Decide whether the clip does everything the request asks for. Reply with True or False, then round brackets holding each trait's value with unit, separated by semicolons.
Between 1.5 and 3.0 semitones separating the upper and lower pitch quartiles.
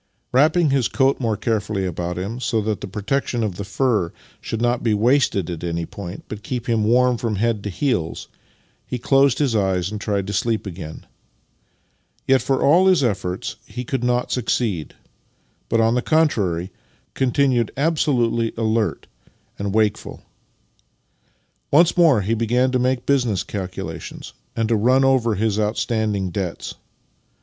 False (4.1 semitones)